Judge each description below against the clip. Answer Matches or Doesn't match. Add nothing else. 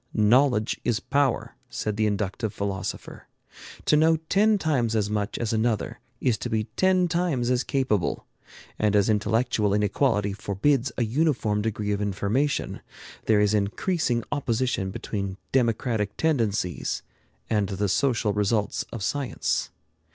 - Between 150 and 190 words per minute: Doesn't match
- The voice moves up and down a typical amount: Matches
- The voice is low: Matches